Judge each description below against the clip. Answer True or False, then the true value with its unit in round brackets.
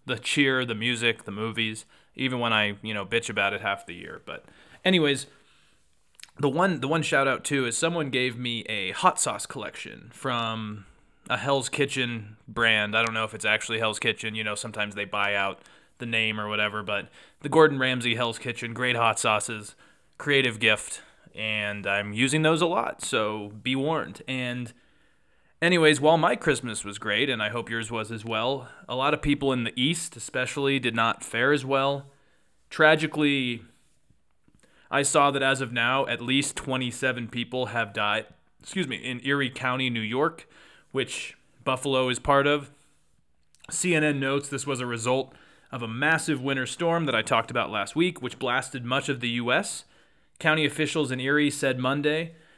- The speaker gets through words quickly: False (180 wpm)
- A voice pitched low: True (125 Hz)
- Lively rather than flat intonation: False (3.8 semitones)